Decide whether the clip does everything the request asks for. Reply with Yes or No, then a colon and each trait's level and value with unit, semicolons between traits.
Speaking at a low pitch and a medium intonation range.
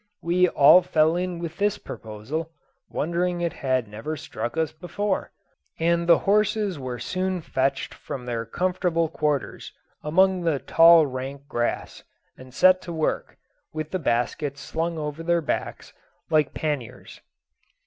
No: medium, 160 Hz; average, 4.2 semitones